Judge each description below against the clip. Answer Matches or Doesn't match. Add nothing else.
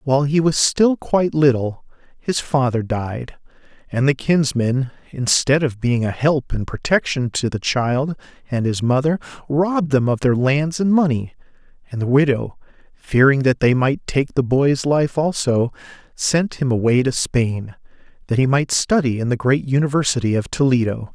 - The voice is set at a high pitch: Doesn't match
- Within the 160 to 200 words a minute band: Matches